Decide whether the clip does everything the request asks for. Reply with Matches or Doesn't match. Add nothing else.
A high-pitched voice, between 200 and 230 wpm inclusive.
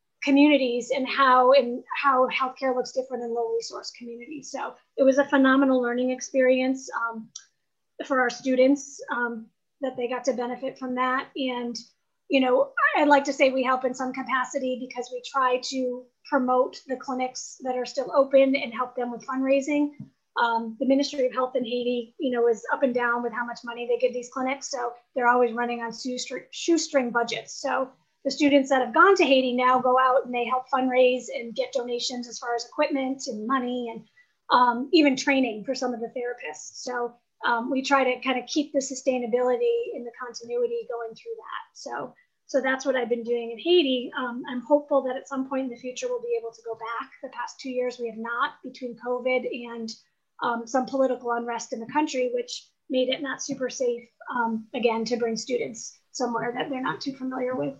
Matches